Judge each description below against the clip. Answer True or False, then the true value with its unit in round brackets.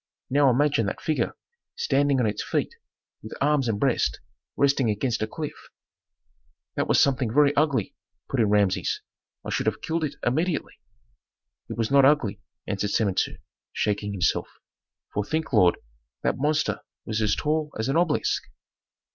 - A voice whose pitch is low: True (130 Hz)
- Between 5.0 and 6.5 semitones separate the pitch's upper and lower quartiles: True (5.6 semitones)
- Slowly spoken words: False (155 wpm)